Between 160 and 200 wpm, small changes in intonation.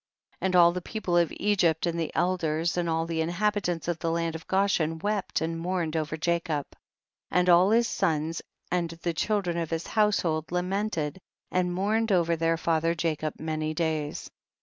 Yes: average, 175 wpm; narrow, 2.1 semitones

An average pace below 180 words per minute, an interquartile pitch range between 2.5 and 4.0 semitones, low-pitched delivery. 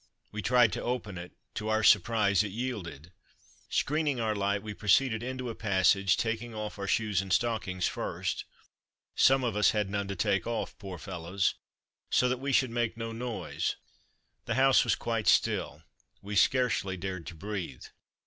Yes: average, 170 wpm; average, 3.5 semitones; low, 105 Hz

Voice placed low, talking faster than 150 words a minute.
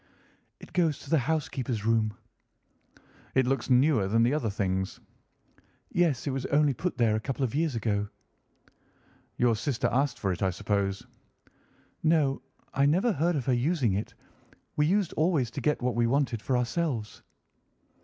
Yes: low, 130 Hz; average, 165 wpm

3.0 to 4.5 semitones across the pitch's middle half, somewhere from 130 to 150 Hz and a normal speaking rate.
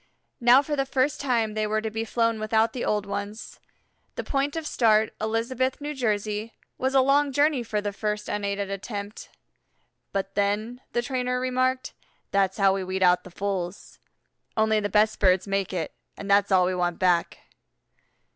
No: average, 4.0 semitones; high, 215 Hz; average, 175 wpm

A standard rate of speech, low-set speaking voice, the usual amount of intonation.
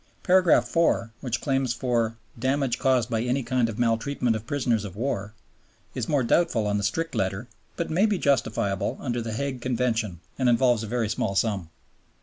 Yes: average, 180 wpm; low, 120 Hz; average, 3.3 semitones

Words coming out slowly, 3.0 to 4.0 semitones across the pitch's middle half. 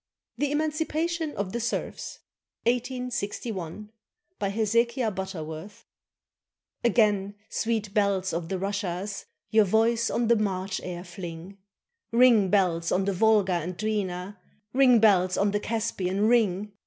Yes: slow, 120 wpm; average, 3.7 semitones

